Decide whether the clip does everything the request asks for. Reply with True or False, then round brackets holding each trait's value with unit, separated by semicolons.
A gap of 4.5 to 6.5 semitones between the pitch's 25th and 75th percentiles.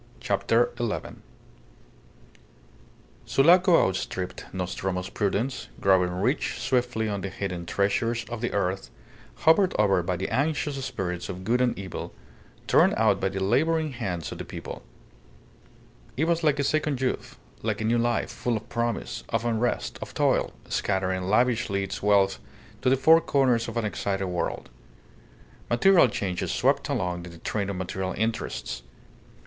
True (4.9 semitones)